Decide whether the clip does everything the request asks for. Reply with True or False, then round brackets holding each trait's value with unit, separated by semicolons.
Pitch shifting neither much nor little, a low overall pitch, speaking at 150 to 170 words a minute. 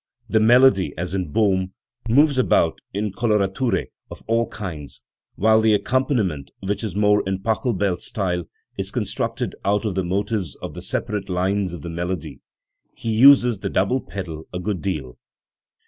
True (3.6 semitones; 100 Hz; 165 wpm)